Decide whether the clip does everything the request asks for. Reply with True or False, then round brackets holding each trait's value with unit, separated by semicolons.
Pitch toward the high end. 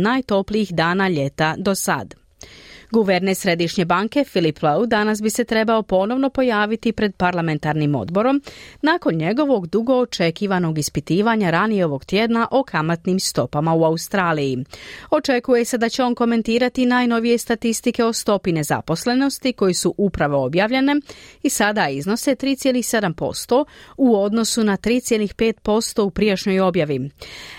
True (210 Hz)